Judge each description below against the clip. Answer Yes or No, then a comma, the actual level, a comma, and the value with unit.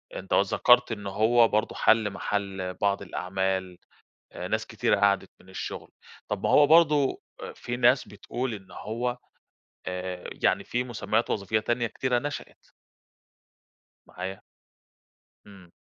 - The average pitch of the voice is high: No, low, 105 Hz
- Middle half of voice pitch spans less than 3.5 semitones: No, average, 4.1 semitones